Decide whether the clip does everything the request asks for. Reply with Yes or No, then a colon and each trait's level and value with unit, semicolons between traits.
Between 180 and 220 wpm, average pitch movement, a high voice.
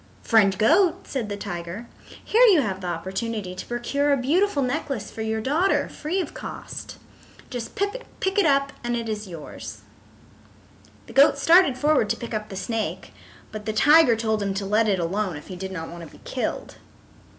No: average, 190 wpm; wide, 6.4 semitones; high, 225 Hz